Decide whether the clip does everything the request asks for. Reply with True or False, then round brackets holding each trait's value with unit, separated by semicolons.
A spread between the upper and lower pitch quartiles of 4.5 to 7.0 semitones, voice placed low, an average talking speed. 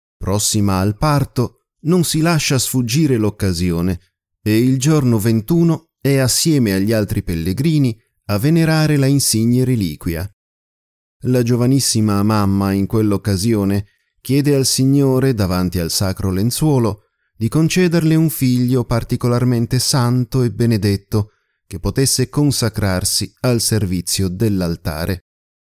False (5.2 semitones; 115 Hz; 110 wpm)